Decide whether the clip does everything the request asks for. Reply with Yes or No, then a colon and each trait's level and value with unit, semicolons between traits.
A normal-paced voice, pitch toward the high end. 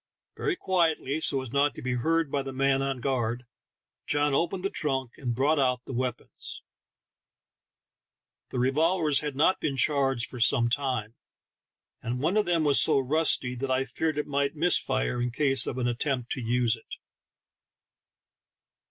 No: average, 170 wpm; low, 135 Hz